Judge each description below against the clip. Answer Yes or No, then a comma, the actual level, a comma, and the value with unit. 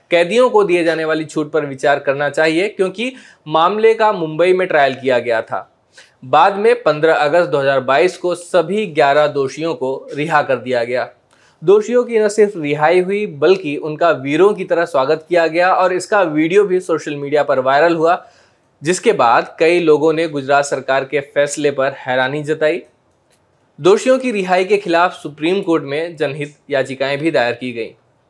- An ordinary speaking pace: Yes, average, 175 wpm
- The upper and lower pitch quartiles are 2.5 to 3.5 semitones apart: No, average, 4.2 semitones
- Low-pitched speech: No, medium, 160 Hz